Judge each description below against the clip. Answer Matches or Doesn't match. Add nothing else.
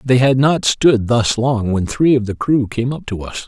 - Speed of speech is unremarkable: Doesn't match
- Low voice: Matches